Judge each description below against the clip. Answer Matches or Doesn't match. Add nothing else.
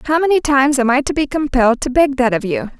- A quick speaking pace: Matches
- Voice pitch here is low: Doesn't match